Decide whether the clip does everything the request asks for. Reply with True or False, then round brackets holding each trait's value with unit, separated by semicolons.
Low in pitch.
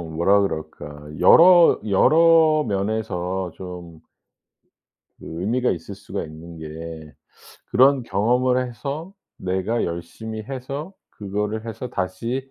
True (105 Hz)